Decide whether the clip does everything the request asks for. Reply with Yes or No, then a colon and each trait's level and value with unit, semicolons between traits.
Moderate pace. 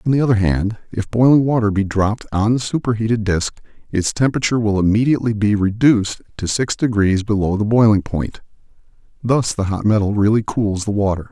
Yes: average, 180 wpm